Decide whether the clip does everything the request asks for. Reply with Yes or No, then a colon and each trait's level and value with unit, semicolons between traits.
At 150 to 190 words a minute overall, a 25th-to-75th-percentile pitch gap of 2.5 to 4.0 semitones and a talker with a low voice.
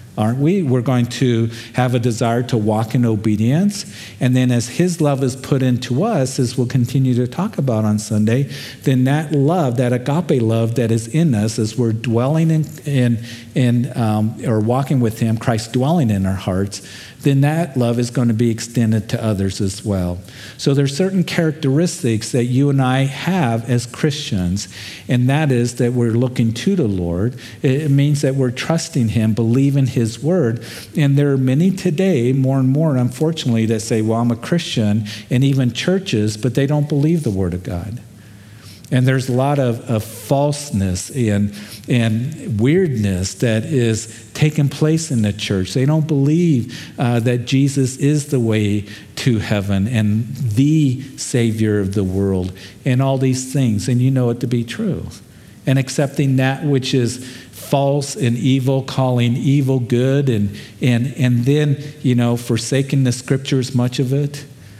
Yes: average, 175 wpm; average, 3.7 semitones; low, 125 Hz